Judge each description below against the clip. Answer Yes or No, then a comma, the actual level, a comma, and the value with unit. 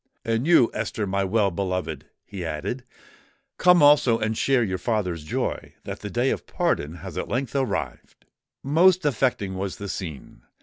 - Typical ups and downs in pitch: No, wide, 6.1 semitones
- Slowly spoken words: No, average, 165 wpm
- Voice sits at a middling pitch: No, low, 110 Hz